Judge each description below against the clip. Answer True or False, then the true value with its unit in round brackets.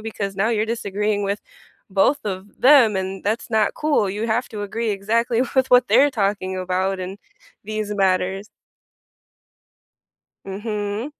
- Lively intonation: False (2.8 semitones)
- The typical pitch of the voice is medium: False (210 Hz)